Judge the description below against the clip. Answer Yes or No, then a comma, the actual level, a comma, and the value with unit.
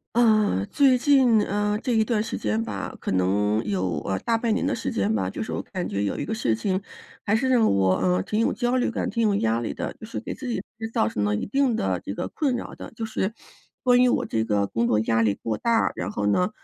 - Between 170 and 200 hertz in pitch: Yes, medium, 185 Hz